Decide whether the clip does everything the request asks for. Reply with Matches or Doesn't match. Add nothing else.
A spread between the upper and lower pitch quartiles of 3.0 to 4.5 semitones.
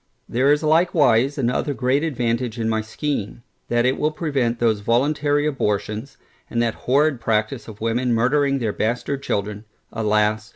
Matches